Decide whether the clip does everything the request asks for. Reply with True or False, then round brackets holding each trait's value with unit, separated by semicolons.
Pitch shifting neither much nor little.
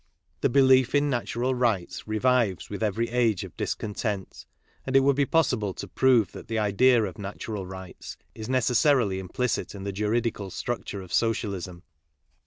True (4.1 semitones)